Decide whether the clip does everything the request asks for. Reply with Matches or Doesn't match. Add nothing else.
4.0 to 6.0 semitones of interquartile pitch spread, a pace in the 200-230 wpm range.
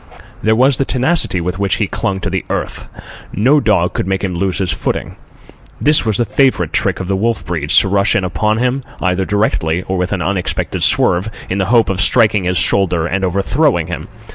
Doesn't match